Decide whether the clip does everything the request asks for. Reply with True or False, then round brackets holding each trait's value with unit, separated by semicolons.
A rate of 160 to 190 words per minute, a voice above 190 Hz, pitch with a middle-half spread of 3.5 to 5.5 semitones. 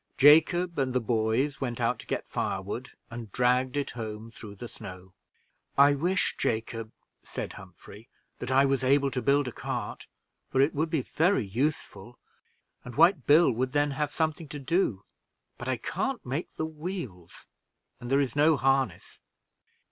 False (165 wpm; 135 Hz; 4.1 semitones)